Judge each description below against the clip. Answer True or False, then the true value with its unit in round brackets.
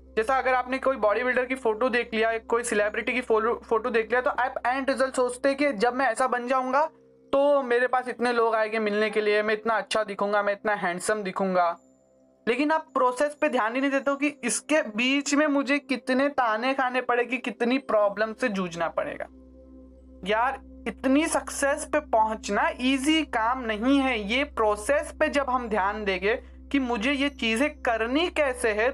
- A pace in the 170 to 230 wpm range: True (190 wpm)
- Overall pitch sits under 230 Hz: False (245 Hz)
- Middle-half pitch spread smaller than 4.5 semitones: True (3.9 semitones)